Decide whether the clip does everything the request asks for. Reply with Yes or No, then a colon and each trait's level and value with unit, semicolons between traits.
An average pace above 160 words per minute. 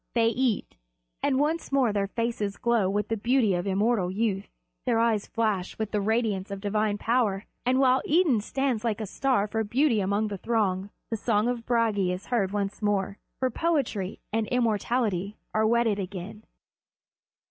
Yes: average, 170 wpm